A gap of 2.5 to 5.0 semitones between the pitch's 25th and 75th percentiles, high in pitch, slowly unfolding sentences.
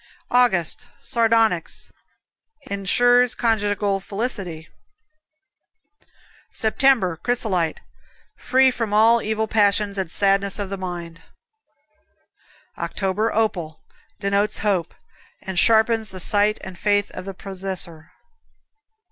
Yes: average, 3.0 semitones; high, 205 Hz; slow, 95 wpm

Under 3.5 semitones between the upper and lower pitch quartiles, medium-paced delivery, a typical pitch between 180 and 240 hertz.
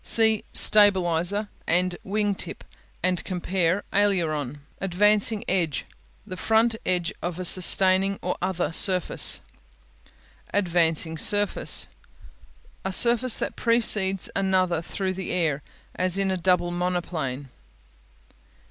No: narrow, 2.6 semitones; slow, 110 wpm; medium, 185 Hz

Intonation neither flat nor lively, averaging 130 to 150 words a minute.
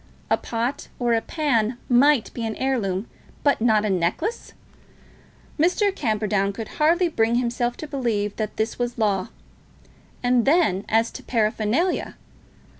Yes: average, 4.1 semitones; average, 140 wpm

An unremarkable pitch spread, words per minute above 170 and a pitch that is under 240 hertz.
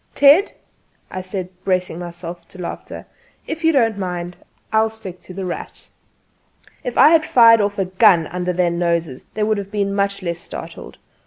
Yes: average, 3.6 semitones; average, 180 wpm; high, 190 Hz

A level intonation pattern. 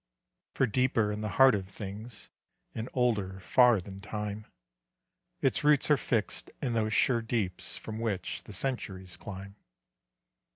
No: average, 3.7 semitones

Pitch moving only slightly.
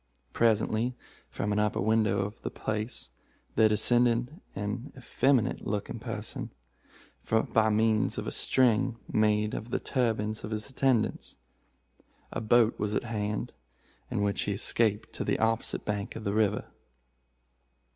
Yes: narrow, 1.9 semitones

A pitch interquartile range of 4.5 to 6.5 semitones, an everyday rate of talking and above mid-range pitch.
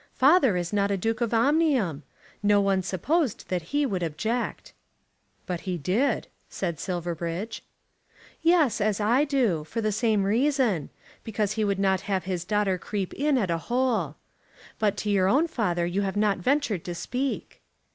Yes: average, 5.1 semitones; average, 165 wpm; high, 205 Hz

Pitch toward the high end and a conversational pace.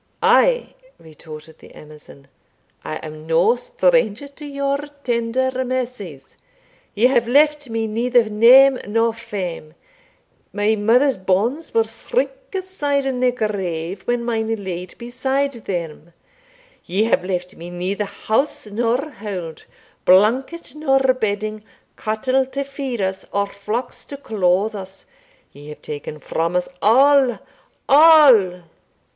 No: high, 225 Hz; slow, 130 wpm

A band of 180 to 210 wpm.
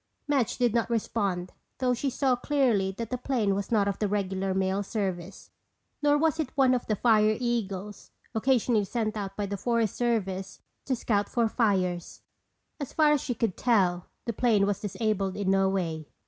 Yes: average, 185 wpm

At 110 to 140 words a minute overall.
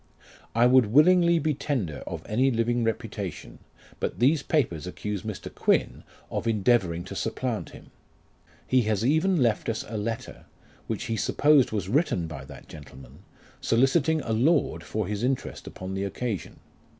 No: average, 155 wpm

